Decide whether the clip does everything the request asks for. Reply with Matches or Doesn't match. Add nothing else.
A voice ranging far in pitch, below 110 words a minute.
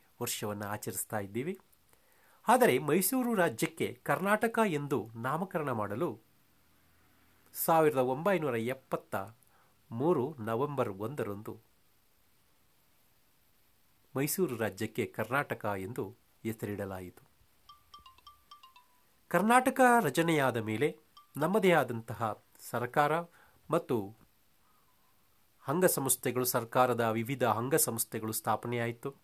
Matches